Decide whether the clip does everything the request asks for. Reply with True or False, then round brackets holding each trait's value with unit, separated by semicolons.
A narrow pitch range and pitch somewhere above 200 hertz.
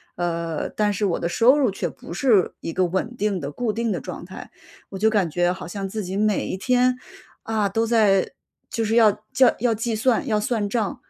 False (3.5 semitones; 210 Hz)